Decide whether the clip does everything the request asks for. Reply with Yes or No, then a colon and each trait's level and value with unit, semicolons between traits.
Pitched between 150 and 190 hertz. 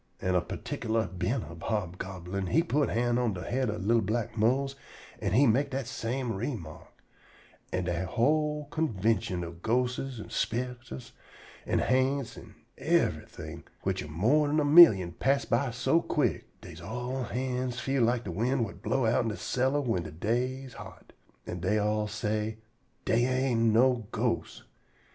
No: low, 115 Hz